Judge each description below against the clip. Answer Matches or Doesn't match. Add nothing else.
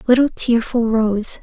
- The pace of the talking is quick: Doesn't match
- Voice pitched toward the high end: Matches